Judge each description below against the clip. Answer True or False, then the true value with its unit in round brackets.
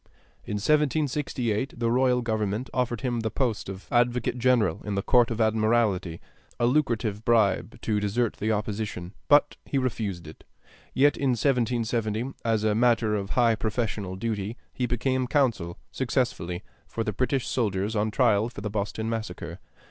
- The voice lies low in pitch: True (115 Hz)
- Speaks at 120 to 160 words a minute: True (155 wpm)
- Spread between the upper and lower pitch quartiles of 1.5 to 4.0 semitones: True (3.0 semitones)